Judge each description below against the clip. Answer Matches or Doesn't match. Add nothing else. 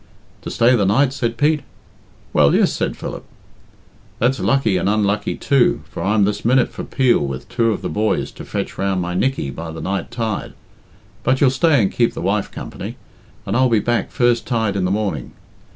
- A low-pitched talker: Matches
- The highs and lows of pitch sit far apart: Doesn't match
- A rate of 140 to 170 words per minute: Doesn't match